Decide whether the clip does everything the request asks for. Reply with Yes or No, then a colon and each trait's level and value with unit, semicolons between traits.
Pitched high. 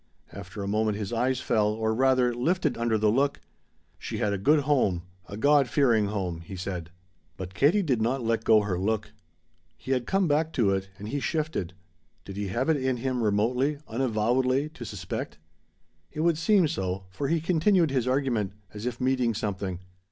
No: low, 120 Hz